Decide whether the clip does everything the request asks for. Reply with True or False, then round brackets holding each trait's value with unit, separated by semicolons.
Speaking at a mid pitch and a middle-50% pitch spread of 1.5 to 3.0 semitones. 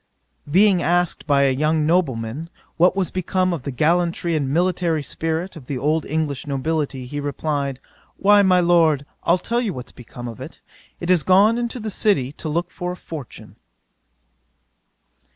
False (160 Hz; 4.2 semitones)